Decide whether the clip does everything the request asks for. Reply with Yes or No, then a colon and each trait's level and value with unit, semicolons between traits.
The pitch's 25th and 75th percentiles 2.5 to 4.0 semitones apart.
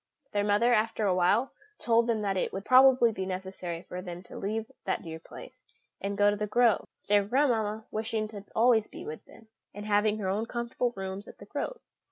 Yes: average, 2.9 semitones